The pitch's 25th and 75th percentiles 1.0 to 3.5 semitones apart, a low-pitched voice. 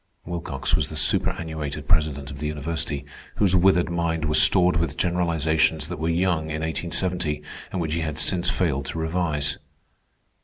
Yes: narrow, 2.4 semitones; very low, 80 Hz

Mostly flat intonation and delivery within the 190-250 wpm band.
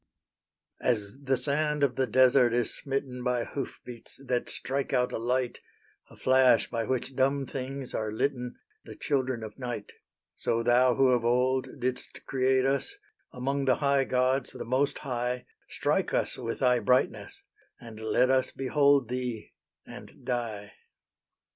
No: narrow, 1.7 semitones; average, 155 wpm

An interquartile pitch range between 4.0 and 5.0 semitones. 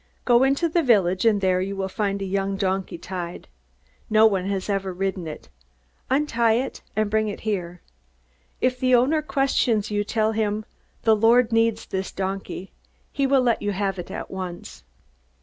No: average, 3.5 semitones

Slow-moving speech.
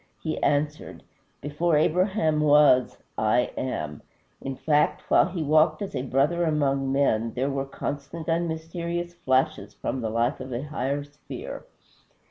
No: average, 145 wpm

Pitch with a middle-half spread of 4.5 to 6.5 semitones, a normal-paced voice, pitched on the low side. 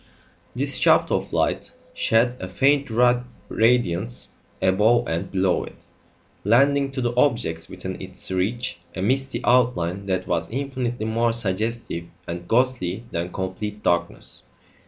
No: average, 4.9 semitones; slow, 130 wpm; low, 110 Hz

